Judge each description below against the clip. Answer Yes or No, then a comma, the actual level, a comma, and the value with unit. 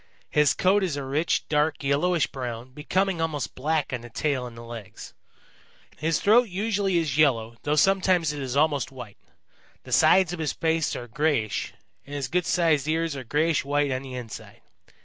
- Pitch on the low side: No, medium, 150 Hz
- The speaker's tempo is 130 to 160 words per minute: No, average, 180 wpm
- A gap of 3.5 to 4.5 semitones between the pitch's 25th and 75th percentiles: Yes, average, 4.2 semitones